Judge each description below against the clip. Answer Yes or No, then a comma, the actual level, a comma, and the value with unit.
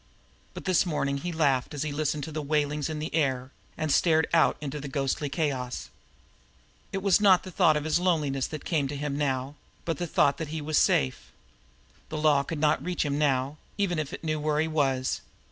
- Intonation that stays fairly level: Yes, narrow, 2.3 semitones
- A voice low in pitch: No, medium, 150 Hz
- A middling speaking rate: No, fast, 215 wpm